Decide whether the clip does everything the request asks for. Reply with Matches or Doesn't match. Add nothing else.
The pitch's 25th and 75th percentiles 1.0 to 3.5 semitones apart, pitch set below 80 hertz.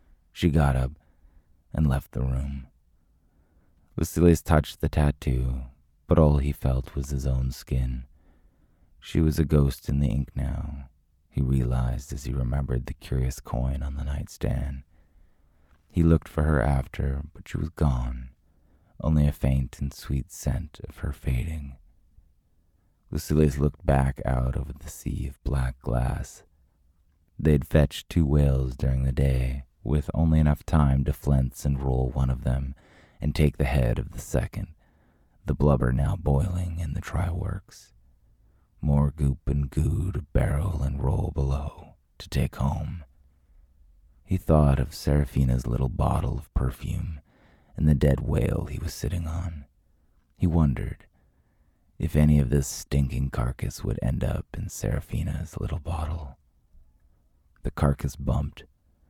Matches